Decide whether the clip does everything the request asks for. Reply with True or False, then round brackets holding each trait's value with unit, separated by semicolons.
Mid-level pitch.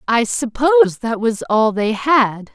False (235 Hz)